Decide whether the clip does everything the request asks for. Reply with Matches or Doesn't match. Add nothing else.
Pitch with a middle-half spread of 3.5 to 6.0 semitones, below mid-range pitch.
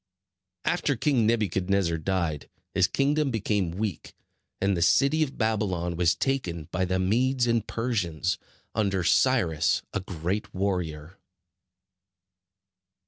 Matches